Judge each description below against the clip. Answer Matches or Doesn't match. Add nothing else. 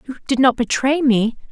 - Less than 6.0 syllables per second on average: Matches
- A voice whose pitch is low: Doesn't match